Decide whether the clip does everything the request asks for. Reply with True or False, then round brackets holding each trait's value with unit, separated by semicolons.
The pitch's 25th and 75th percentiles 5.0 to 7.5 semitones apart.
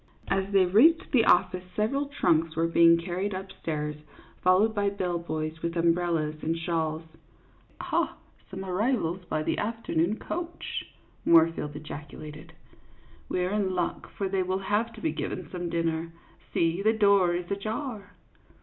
False (3.5 semitones)